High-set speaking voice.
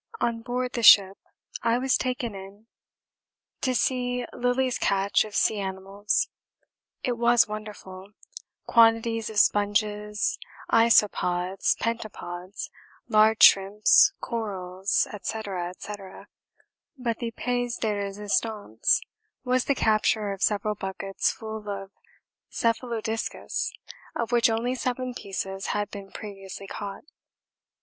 Yes: high, 215 Hz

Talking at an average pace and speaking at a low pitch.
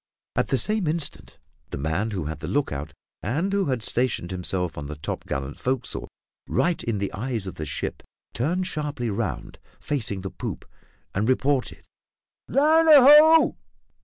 Yes: average, 155 wpm; low, 120 Hz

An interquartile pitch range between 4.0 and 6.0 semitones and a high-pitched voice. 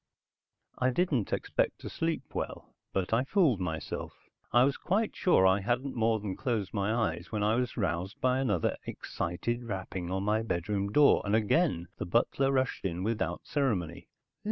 No: average, 5.3 semitones; low, 110 Hz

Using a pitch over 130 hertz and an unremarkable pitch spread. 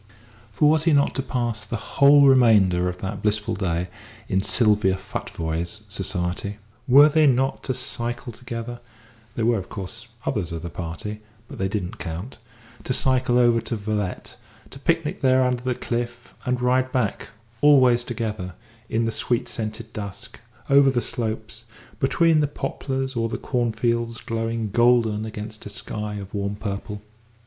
No: low, 115 Hz; average, 3.5 semitones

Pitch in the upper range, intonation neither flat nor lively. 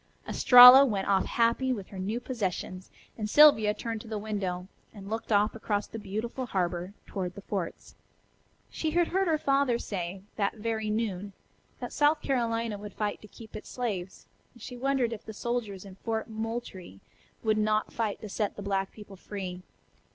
Yes: high, 215 Hz; average, 3.2 semitones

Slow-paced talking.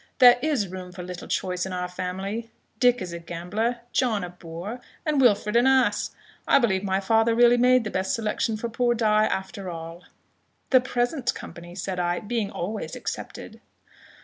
No: average, 175 wpm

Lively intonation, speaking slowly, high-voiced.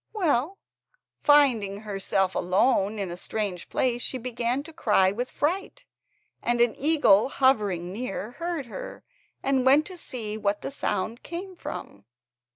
No: wide, 5.8 semitones; average, 150 wpm; high, 240 Hz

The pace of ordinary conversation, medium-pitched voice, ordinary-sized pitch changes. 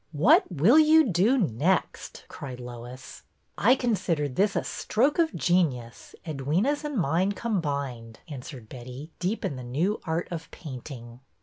No: average, 145 wpm; medium, 160 Hz; wide, 8.4 semitones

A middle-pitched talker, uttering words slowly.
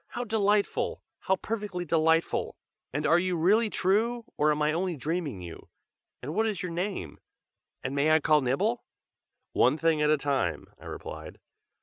No: medium, 165 Hz; average, 165 wpm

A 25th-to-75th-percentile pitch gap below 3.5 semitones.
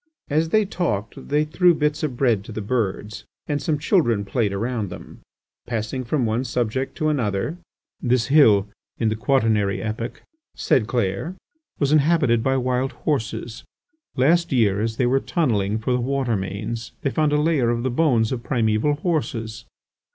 No: average, 5.0 semitones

